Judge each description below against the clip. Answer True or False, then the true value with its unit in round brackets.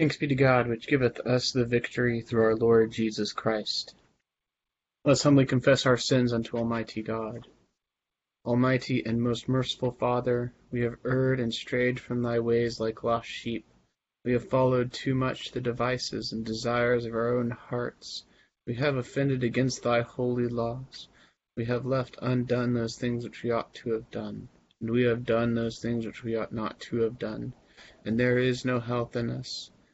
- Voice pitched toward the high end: False (120 Hz)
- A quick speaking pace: False (180 wpm)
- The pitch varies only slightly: True (1.6 semitones)